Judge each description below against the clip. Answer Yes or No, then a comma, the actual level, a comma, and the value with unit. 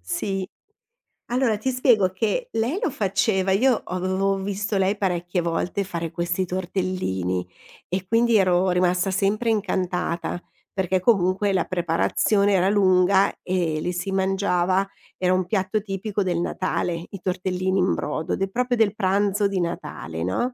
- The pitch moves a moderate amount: No, narrow, 2.1 semitones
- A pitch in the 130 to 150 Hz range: No, high, 190 Hz